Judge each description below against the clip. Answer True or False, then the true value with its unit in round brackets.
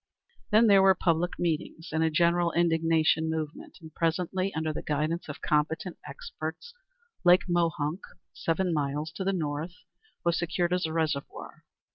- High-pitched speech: False (165 Hz)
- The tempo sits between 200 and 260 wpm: False (150 wpm)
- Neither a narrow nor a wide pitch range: False (2.0 semitones)